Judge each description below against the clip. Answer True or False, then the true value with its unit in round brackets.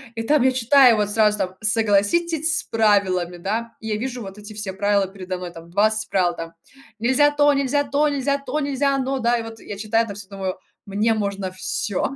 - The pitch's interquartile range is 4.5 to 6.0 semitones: True (4.8 semitones)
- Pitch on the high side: True (220 Hz)